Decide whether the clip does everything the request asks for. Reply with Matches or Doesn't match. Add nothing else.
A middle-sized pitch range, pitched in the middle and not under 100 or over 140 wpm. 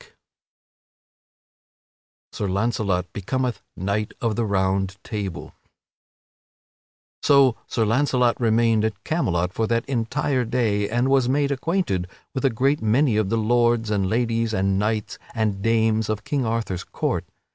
Doesn't match